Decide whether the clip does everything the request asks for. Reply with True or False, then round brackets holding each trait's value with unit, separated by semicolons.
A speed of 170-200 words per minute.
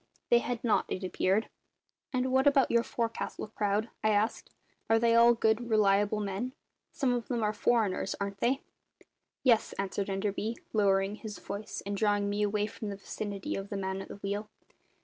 True (180 wpm)